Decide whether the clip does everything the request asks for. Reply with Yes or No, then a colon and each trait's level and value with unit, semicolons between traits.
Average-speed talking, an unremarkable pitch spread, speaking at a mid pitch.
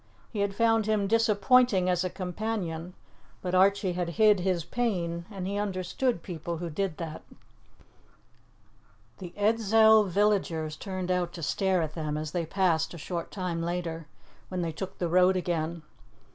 Yes: average, 160 wpm; average, 3.2 semitones; medium, 180 Hz